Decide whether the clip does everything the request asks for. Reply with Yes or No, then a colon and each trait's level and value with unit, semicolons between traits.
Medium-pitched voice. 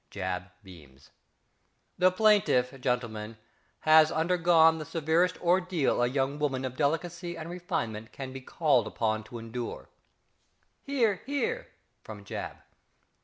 Yes: medium, 145 Hz